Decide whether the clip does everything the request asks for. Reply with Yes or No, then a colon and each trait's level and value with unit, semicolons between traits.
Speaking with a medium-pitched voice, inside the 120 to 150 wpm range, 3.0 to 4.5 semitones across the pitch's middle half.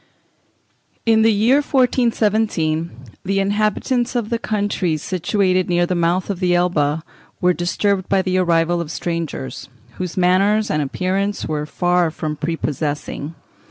Yes: medium, 180 Hz; average, 140 wpm; average, 3.7 semitones